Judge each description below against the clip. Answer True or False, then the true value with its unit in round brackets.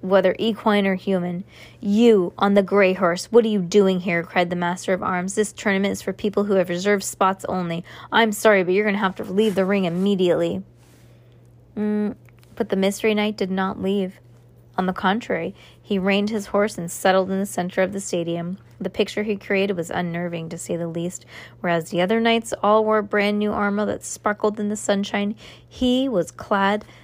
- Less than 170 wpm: False (200 wpm)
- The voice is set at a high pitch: True (195 Hz)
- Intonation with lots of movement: False (2.8 semitones)